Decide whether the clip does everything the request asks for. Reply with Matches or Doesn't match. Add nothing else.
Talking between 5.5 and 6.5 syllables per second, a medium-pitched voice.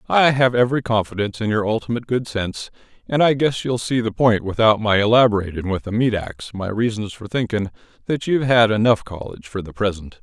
Doesn't match